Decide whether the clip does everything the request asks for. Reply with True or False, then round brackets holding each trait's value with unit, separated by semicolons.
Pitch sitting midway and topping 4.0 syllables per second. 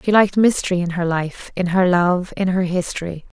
True (180 Hz; 5.3 syllables/s)